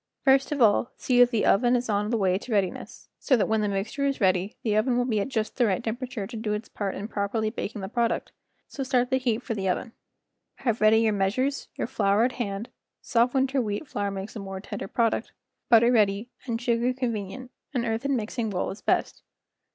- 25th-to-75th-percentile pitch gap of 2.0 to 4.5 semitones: Yes, average, 3.4 semitones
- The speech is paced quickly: Yes, fast, 225 wpm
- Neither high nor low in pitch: No, high, 225 Hz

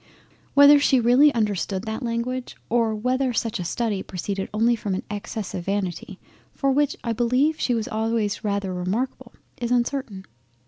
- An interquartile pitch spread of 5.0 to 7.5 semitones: No, average, 3.8 semitones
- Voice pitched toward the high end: Yes, high, 230 Hz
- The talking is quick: No, average, 165 wpm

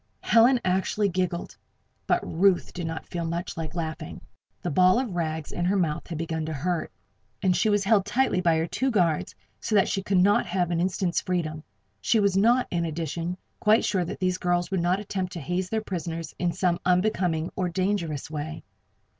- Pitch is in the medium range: Yes, medium, 180 Hz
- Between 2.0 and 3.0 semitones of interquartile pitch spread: Yes, average, 2.7 semitones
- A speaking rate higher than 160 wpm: Yes, average, 200 wpm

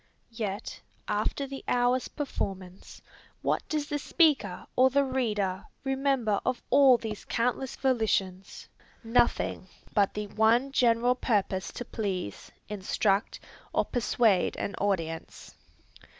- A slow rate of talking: Yes, slow, 115 wpm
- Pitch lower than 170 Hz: No, high, 230 Hz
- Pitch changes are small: No, average, 4.6 semitones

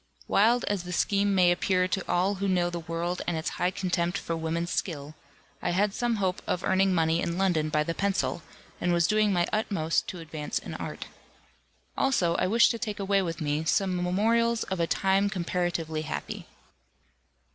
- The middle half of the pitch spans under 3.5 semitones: Yes, average, 2.9 semitones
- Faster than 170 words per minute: Yes, average, 190 wpm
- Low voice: No, medium, 180 Hz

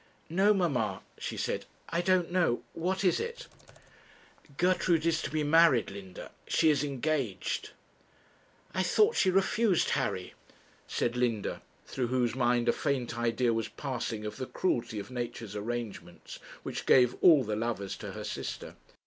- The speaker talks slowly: No, average, 150 wpm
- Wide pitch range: Yes, wide, 6.4 semitones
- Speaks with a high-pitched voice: No, low, 130 Hz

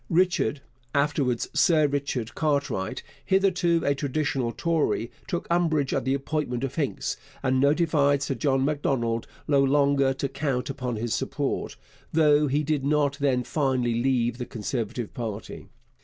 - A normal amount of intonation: Yes, average, 3.1 semitones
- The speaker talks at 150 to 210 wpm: No, average, 140 wpm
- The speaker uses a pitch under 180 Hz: Yes, medium, 140 Hz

